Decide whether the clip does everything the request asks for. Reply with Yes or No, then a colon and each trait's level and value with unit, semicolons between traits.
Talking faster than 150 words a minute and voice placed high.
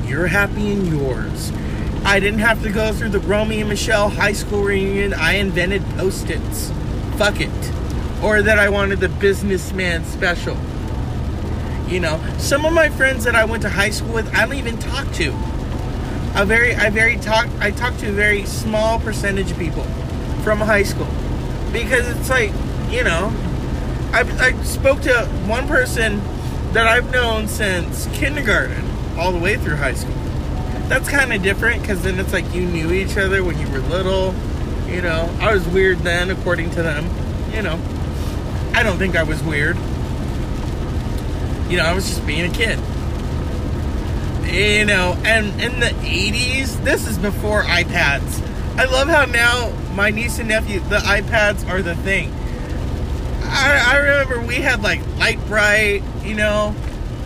No: average, 170 wpm; low, 100 Hz